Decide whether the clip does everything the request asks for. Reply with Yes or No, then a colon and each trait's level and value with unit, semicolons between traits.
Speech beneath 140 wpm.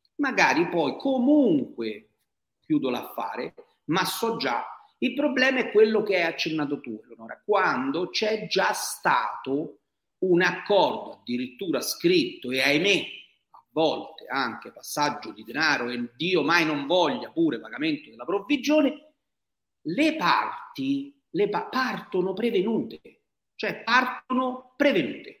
Yes: average, 120 wpm